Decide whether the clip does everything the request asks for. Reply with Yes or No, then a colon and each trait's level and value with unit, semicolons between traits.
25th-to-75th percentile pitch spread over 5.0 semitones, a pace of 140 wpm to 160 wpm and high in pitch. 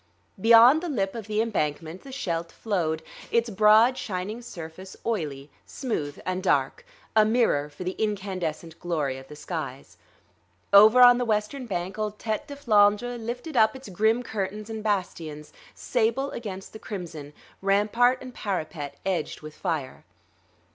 Yes: wide, 5.4 semitones; average, 150 wpm; high, 205 Hz